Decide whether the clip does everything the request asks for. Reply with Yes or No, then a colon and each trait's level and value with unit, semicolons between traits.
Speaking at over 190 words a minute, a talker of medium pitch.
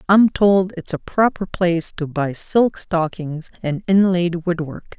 No: average, 170 wpm; medium, 175 Hz